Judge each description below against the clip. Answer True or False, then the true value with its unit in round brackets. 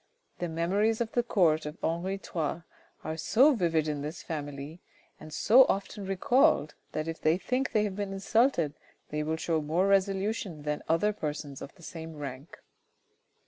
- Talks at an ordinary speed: True (170 wpm)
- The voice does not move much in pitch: False (4.6 semitones)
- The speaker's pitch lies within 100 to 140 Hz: False (170 Hz)